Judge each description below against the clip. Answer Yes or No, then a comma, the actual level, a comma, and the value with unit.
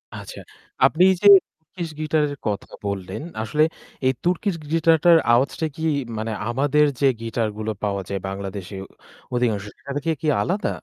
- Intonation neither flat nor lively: No, wide, 7.2 semitones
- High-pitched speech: No, low, 135 Hz